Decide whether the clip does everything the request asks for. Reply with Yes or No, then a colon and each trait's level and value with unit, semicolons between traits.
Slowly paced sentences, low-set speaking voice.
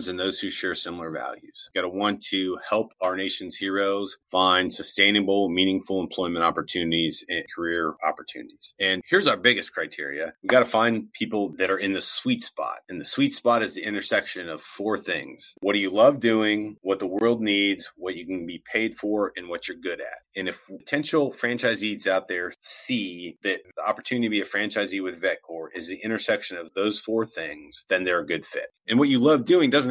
No: fast, 205 wpm; low, 100 Hz